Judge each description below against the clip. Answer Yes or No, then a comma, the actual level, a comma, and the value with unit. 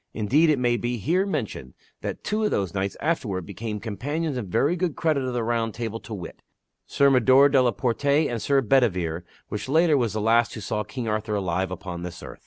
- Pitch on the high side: No, low, 120 Hz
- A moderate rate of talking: No, fast, 215 wpm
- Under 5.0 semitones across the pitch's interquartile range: No, wide, 5.4 semitones